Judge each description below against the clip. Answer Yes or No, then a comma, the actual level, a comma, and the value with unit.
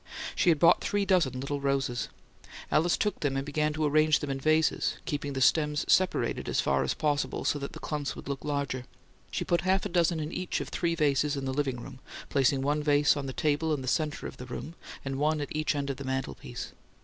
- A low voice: No, medium, 145 Hz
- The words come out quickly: Yes, fast, 230 wpm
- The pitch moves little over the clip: Yes, narrow, 2.3 semitones